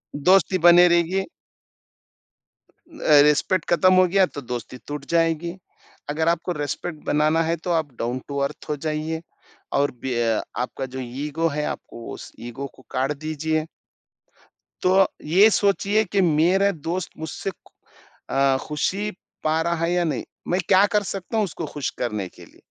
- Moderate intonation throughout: Yes, average, 3.9 semitones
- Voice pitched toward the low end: No, medium, 160 Hz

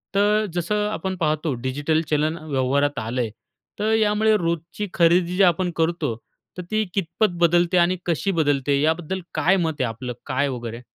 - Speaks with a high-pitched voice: No, medium, 165 Hz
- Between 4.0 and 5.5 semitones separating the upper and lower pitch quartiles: Yes, average, 4.7 semitones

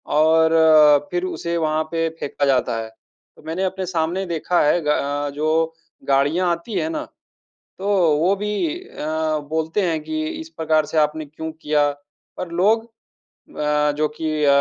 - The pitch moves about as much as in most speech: Yes, average, 3.0 semitones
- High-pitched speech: No, medium, 160 Hz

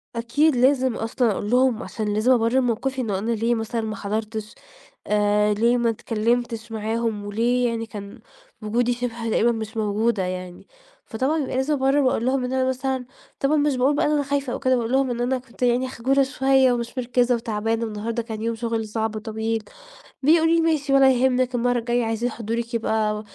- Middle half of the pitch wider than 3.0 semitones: No, average, 2.7 semitones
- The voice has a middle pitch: No, high, 235 Hz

